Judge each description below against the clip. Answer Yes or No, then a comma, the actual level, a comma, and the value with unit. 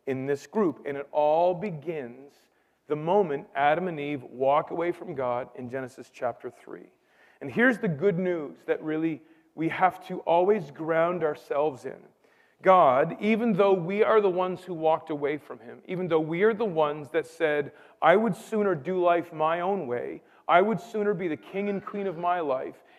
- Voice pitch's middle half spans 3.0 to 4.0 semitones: No, average, 4.6 semitones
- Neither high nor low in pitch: Yes, medium, 170 Hz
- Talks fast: No, average, 190 wpm